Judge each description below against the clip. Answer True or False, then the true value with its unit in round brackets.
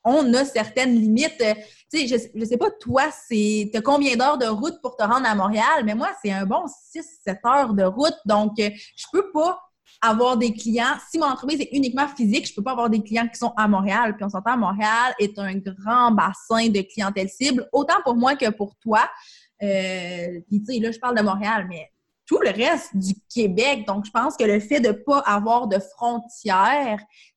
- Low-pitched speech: False (225 Hz)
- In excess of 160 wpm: True (220 wpm)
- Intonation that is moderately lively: True (3.9 semitones)